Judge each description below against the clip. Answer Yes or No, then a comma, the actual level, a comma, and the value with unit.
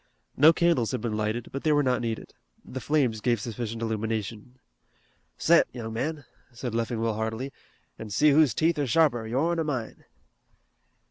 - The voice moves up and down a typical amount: Yes, average, 4.6 semitones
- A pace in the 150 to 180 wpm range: Yes, average, 160 wpm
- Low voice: Yes, low, 120 Hz